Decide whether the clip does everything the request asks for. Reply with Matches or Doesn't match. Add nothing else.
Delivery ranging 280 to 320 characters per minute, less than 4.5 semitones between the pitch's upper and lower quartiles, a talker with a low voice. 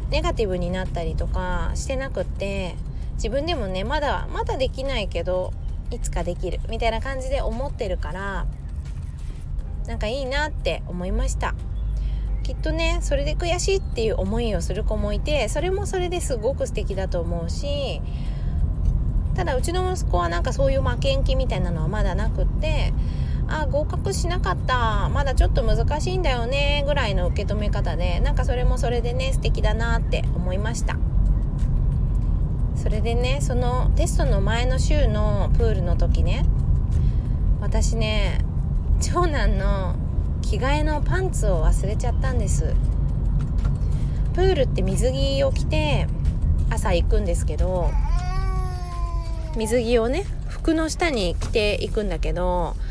Matches